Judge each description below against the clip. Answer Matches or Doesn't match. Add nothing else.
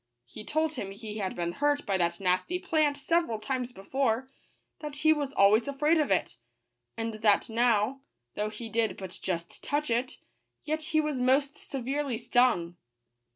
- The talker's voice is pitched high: Matches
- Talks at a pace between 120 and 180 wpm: Matches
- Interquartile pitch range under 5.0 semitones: Doesn't match